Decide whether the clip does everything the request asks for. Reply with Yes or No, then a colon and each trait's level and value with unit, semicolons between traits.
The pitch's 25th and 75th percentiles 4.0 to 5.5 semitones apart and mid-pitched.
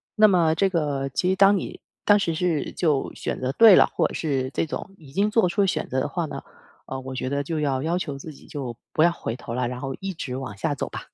Yes: average, 5.2 semitones; medium, 155 Hz